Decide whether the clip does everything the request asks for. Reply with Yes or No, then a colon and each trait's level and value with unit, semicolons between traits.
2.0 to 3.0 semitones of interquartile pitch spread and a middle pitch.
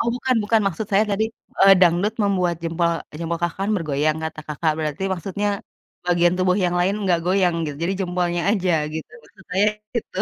Yes: narrow, 2.6 semitones; medium, 180 Hz